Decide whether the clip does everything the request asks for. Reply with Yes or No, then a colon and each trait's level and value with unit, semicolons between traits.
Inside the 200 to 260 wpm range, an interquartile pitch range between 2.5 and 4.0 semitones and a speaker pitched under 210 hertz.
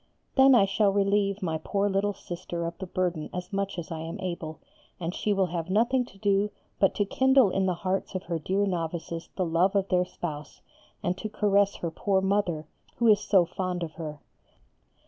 Yes: fast, 205 wpm; average, 2.9 semitones; high, 190 Hz